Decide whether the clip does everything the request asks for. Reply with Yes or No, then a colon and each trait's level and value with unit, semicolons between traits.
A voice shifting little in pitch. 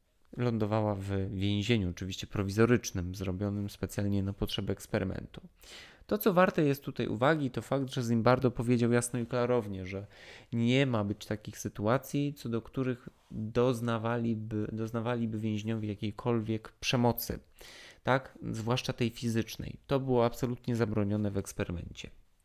No: average, 3.2 semitones